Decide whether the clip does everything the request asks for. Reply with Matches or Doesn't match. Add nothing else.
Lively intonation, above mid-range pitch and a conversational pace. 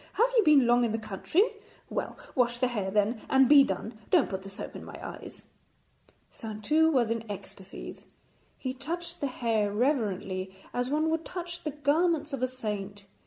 Matches